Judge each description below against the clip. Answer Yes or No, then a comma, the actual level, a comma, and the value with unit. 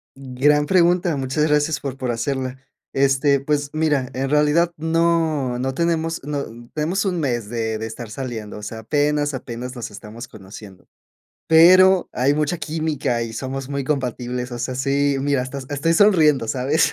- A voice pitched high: No, medium, 140 Hz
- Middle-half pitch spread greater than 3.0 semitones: Yes, average, 3.7 semitones